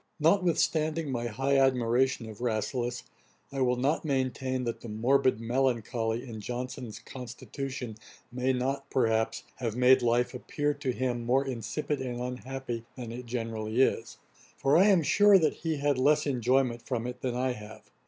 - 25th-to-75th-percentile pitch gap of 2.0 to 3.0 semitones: Yes, narrow, 2.4 semitones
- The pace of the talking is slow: No, average, 160 wpm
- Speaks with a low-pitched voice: Yes, low, 125 Hz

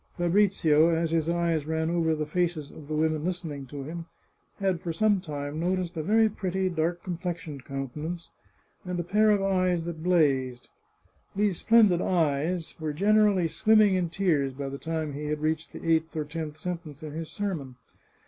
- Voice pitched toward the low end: No, medium, 165 Hz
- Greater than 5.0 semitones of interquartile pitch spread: No, average, 3.0 semitones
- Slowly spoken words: No, average, 180 wpm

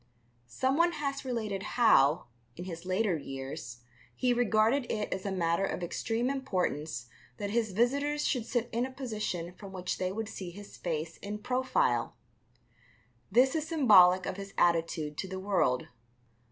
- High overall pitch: Yes, high, 200 Hz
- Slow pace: No, average, 155 wpm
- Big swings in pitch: Yes, wide, 5.9 semitones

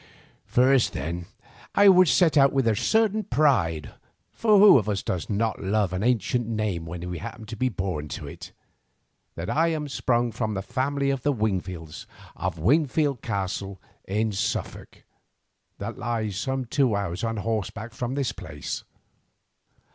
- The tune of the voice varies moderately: No, wide, 6.0 semitones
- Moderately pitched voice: No, low, 115 Hz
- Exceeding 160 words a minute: No, average, 155 wpm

